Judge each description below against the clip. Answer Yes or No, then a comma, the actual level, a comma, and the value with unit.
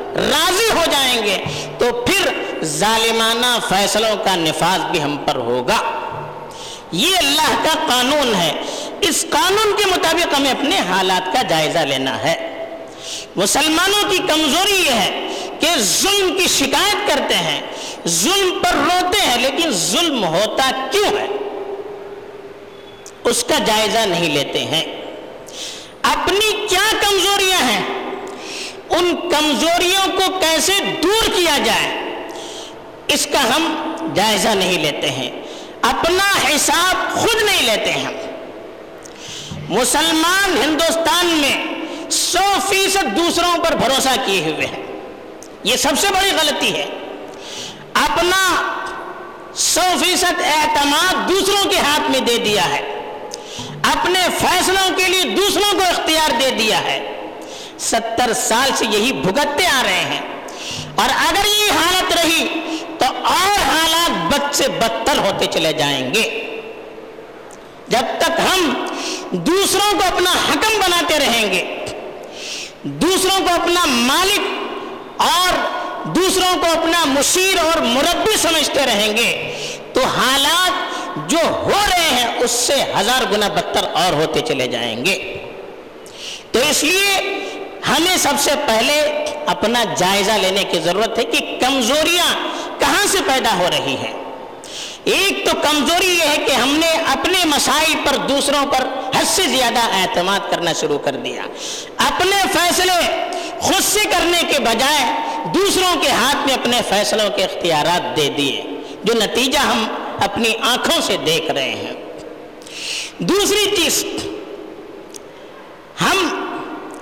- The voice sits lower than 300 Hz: No, very high, 345 Hz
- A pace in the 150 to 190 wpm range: No, average, 130 wpm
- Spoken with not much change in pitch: No, average, 5.0 semitones